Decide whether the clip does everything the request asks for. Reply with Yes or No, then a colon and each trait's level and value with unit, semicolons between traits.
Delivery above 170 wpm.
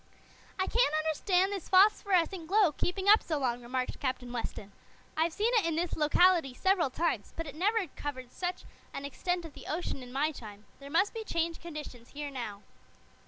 Yes: average, 185 wpm